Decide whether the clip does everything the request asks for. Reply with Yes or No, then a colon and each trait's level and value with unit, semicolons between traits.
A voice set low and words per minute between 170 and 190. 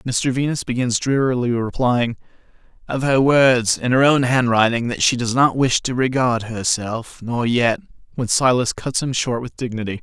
Yes: low, 125 Hz; average, 175 wpm